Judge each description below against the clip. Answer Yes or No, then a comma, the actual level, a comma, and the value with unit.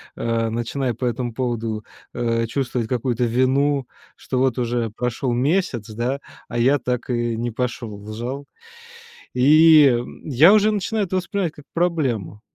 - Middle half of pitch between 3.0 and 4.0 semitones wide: Yes, average, 3.3 semitones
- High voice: No, low, 125 Hz